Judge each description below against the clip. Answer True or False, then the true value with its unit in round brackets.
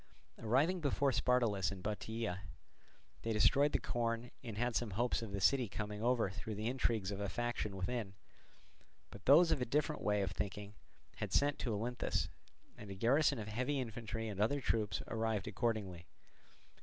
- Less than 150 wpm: False (170 wpm)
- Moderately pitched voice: False (115 Hz)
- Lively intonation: False (3.3 semitones)